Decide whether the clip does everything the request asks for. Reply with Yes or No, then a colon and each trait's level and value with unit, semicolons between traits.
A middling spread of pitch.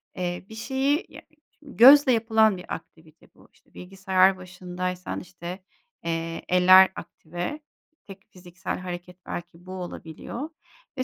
Yes: average, 3.8 semitones